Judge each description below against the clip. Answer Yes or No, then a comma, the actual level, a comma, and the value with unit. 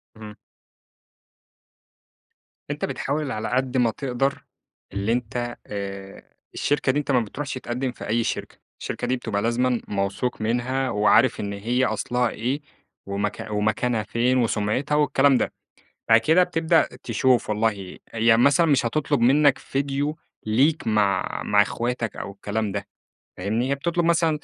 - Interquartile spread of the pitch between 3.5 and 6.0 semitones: Yes, average, 4.1 semitones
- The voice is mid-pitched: No, low, 120 Hz